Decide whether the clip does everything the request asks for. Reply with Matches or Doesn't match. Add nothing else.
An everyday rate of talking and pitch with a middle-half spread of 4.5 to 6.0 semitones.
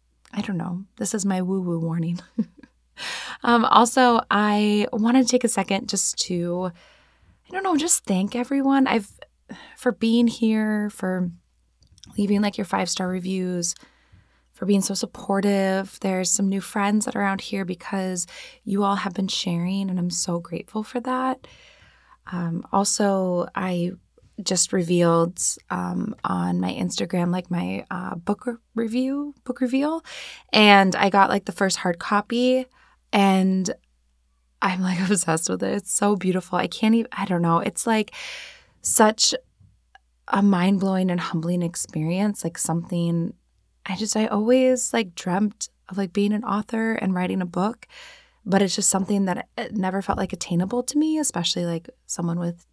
Doesn't match